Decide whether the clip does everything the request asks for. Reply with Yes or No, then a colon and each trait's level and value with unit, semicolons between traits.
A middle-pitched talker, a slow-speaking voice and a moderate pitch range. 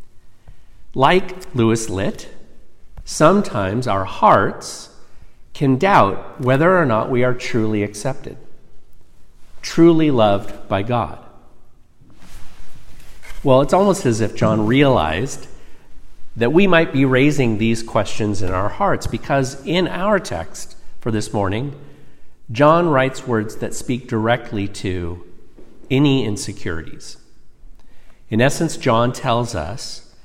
No: low, 120 Hz; slow, 115 wpm; average, 4.8 semitones